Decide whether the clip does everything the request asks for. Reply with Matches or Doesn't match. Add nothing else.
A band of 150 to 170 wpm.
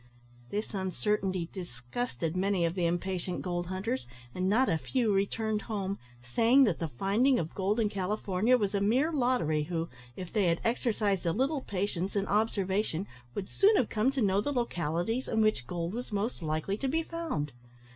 Doesn't match